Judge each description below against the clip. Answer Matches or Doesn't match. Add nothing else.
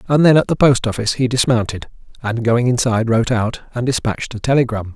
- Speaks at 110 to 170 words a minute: Doesn't match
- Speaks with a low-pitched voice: Matches